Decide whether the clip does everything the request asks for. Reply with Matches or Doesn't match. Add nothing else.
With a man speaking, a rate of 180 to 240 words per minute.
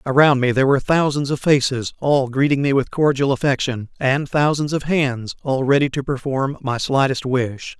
Matches